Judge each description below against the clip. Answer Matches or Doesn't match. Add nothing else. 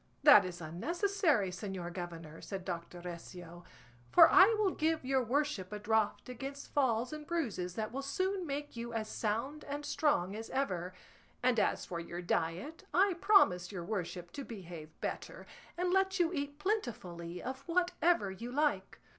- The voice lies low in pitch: Doesn't match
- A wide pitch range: Matches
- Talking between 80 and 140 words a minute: Doesn't match